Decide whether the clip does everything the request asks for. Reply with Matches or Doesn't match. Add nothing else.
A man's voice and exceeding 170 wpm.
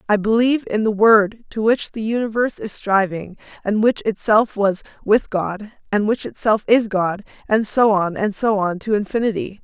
Doesn't match